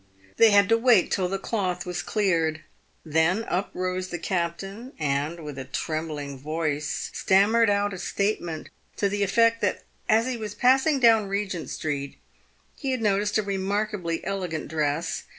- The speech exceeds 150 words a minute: Yes, average, 160 wpm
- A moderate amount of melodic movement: Yes, average, 4.5 semitones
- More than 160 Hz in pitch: Yes, high, 190 Hz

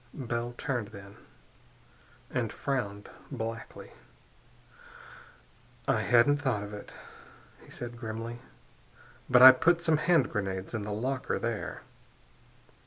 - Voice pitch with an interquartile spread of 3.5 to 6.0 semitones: Yes, average, 3.8 semitones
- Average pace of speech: No, slow, 110 wpm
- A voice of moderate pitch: No, low, 120 Hz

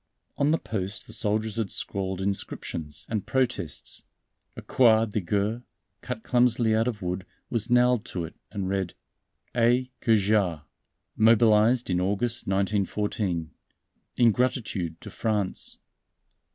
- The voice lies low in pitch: Yes, low, 105 Hz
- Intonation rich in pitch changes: No, average, 3.3 semitones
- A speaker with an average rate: No, slow, 125 wpm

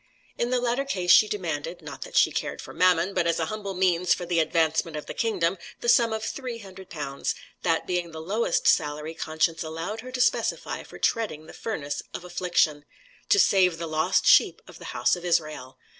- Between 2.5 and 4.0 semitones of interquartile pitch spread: No, average, 4.6 semitones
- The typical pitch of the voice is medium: Yes, medium, 175 Hz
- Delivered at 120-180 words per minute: No, average, 200 wpm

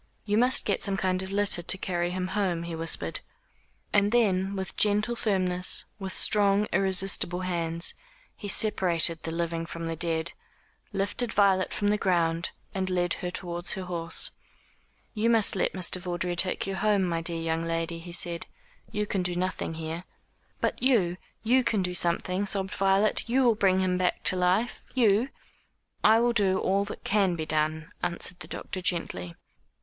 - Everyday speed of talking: Yes, average, 175 wpm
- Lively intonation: No, average, 2.8 semitones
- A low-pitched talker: No, medium, 185 Hz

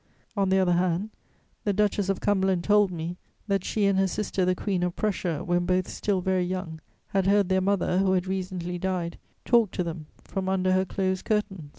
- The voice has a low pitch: No, medium, 185 Hz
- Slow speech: No, fast, 205 wpm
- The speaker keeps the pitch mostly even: Yes, narrow, 1.7 semitones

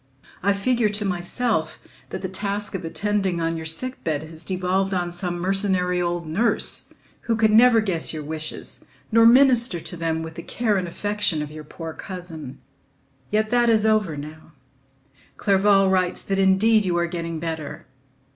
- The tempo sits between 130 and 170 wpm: Yes, average, 165 wpm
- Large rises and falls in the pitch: No, average, 4.1 semitones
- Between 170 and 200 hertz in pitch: Yes, medium, 185 Hz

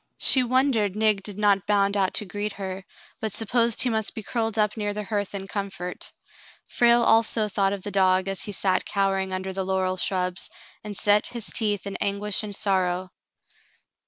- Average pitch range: No, narrow, 2.0 semitones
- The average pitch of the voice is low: No, high, 200 Hz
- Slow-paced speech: No, average, 190 wpm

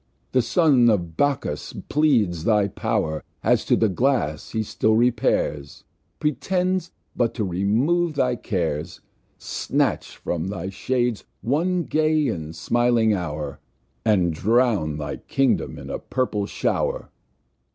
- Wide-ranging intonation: Yes, wide, 7.9 semitones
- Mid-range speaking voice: No, low, 115 Hz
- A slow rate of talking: Yes, slow, 125 wpm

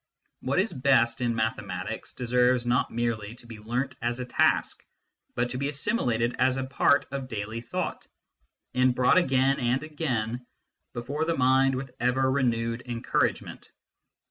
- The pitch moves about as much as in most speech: No, narrow, 2.1 semitones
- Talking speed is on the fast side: No, average, 150 wpm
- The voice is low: Yes, low, 125 Hz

